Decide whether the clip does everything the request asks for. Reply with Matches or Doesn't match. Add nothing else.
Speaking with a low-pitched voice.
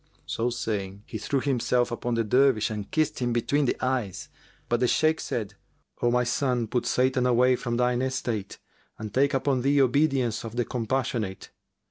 Matches